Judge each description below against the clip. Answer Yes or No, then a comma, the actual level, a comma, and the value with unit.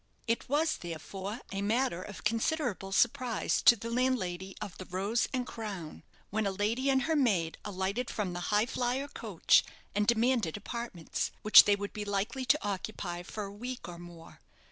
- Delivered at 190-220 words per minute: No, average, 170 wpm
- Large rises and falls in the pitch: No, average, 4.3 semitones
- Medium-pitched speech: No, high, 210 Hz